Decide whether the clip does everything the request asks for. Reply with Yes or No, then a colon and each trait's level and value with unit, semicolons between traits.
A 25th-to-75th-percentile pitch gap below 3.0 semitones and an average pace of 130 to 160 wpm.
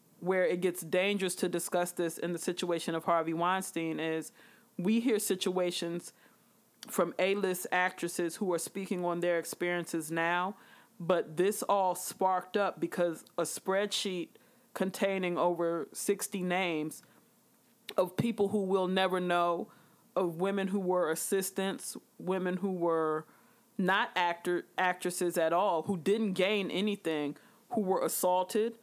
Yes: narrow, 2.5 semitones; slow, 135 wpm